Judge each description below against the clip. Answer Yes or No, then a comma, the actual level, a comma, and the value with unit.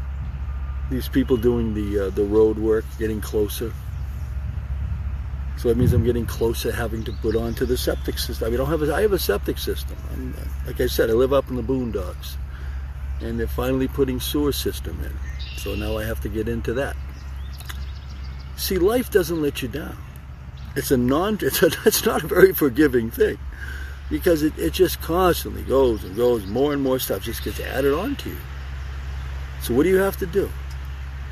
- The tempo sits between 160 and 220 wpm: Yes, average, 200 wpm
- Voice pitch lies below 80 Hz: Yes, very low, 70 Hz